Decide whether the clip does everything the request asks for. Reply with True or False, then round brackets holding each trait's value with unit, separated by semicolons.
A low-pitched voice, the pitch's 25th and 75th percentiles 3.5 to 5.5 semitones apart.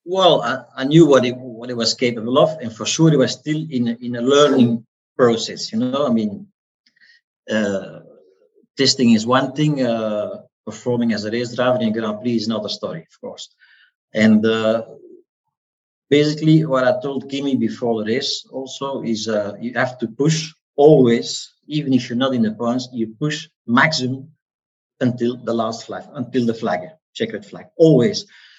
True (125 Hz; 4.5 semitones)